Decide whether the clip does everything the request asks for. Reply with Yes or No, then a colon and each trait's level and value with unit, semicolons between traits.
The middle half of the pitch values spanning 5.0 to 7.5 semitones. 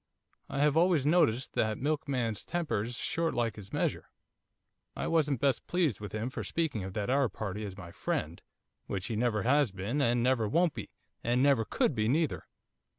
Yes: wide, 5.5 semitones